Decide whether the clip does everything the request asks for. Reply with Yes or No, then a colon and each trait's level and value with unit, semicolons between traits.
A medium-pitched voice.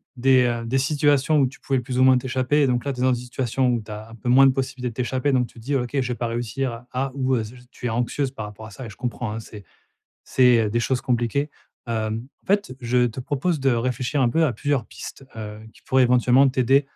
No: low, 125 Hz